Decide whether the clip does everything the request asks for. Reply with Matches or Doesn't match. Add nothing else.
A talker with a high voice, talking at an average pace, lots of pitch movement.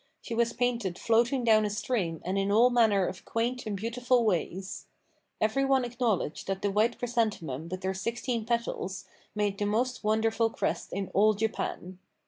Doesn't match